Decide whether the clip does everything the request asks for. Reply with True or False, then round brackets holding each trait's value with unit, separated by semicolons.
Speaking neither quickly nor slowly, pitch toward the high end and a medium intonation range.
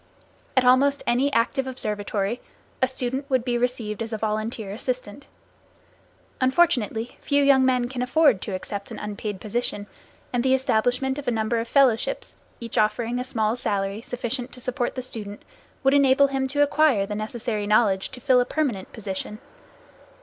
True (165 wpm; 245 Hz; 3.6 semitones)